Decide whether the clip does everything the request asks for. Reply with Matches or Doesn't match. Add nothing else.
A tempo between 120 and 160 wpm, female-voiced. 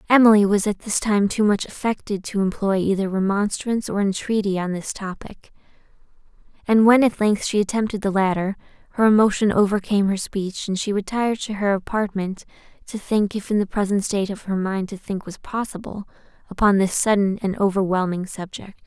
Doesn't match